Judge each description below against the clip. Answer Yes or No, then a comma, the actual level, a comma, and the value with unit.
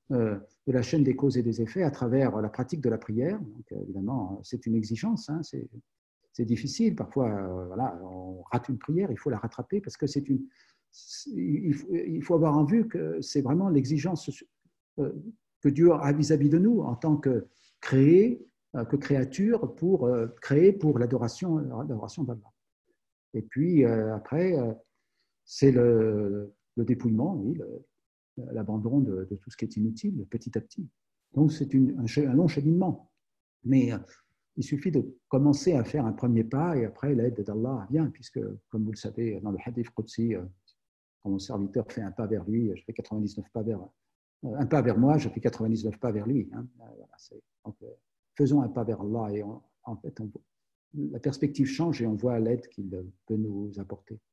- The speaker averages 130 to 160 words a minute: No, average, 200 wpm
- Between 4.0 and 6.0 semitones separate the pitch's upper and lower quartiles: Yes, average, 4.7 semitones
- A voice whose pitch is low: Yes, low, 125 Hz